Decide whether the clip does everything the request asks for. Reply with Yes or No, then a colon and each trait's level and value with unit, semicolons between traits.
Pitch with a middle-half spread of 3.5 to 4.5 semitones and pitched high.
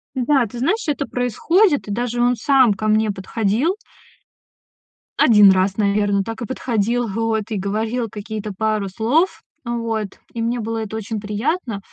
No: average, 2.9 semitones; high, 225 Hz